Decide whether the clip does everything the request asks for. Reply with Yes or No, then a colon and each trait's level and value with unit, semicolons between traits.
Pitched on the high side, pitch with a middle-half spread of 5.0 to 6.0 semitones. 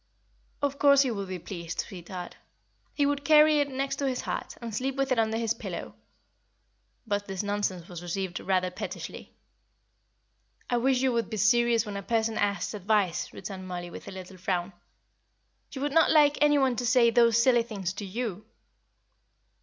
Yes: high, 225 Hz; wide, 5.5 semitones